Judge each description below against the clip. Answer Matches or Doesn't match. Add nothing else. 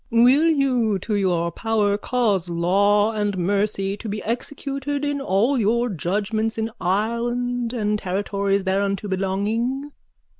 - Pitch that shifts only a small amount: Doesn't match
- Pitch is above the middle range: Matches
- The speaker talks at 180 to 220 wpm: Doesn't match